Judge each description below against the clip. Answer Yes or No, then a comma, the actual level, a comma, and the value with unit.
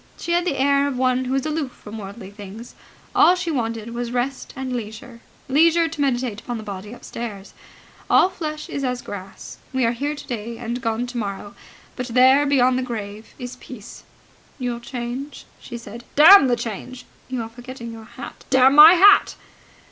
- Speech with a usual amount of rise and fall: Yes, average, 3.2 semitones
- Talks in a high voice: Yes, high, 245 Hz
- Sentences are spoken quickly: No, average, 180 wpm